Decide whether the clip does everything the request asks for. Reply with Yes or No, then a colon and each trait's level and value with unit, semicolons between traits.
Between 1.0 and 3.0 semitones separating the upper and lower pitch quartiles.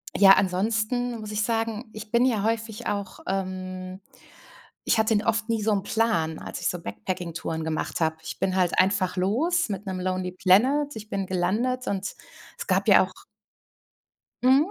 No: average, 3.5 semitones